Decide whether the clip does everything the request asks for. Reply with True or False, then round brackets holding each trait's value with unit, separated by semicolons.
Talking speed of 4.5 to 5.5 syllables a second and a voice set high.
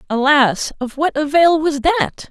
False (3.9 syllables/s; 295 Hz)